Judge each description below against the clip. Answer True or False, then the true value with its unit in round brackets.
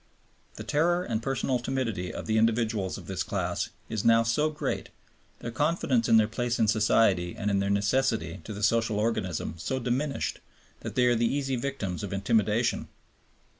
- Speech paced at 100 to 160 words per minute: False (175 wpm)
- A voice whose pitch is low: True (115 Hz)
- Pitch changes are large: False (3.5 semitones)